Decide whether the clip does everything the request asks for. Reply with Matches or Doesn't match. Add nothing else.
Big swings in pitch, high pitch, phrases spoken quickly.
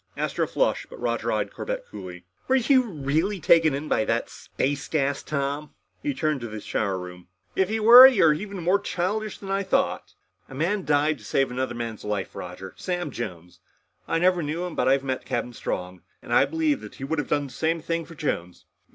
Doesn't match